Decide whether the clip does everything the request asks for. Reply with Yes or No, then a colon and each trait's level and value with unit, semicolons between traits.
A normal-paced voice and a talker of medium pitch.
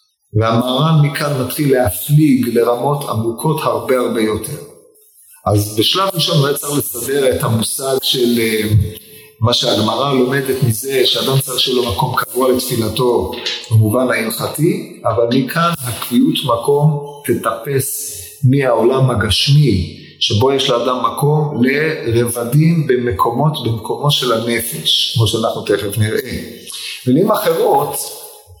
No: average, 115 wpm; low, 130 Hz